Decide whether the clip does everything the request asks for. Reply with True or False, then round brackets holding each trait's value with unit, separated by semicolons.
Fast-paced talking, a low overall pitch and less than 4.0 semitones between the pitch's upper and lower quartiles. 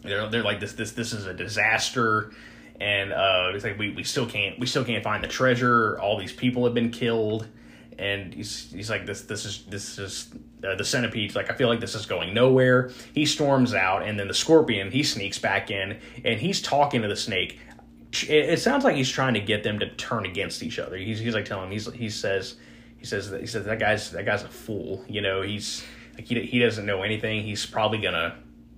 True (230 wpm; 110 Hz; 3.1 semitones)